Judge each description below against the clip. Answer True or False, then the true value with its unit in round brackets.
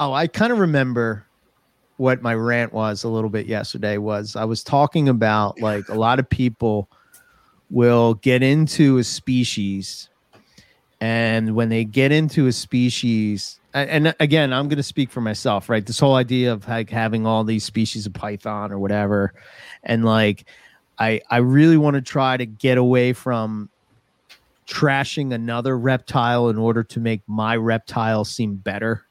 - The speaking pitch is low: True (115 Hz)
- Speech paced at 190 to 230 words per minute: False (165 wpm)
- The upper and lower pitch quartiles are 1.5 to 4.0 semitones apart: True (3.2 semitones)